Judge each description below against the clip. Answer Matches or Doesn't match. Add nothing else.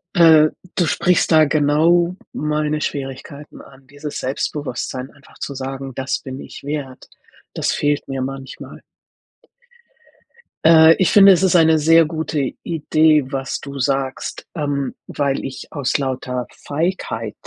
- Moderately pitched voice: Matches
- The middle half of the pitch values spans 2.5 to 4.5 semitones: Matches